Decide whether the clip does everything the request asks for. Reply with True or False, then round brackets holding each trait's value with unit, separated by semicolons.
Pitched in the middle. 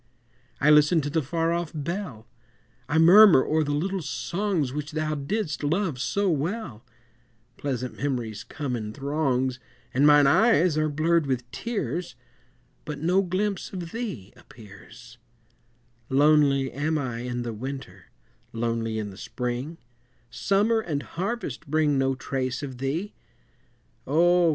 True (145 Hz)